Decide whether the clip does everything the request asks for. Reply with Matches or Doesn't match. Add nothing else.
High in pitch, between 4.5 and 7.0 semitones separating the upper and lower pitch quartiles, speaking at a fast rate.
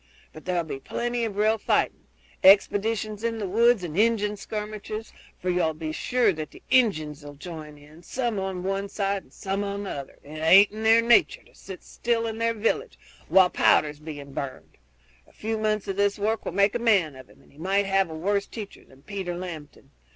Matches